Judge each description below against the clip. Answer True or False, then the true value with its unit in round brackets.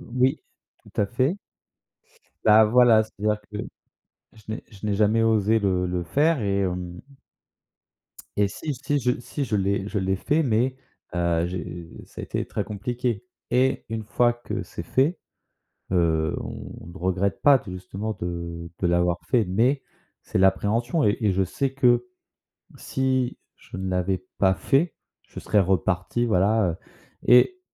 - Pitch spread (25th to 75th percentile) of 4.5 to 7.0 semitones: True (5.0 semitones)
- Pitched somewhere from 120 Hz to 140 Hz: False (105 Hz)